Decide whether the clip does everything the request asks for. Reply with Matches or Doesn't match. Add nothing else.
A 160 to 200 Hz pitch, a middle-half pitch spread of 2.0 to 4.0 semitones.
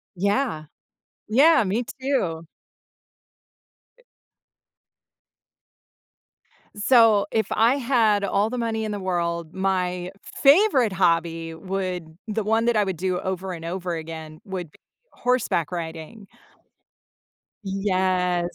Doesn't match